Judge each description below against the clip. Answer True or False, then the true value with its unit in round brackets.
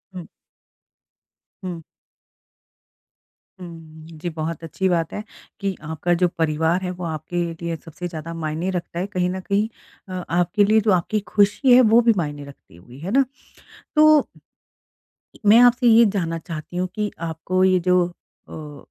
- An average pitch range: True (3.6 semitones)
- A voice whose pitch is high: False (175 Hz)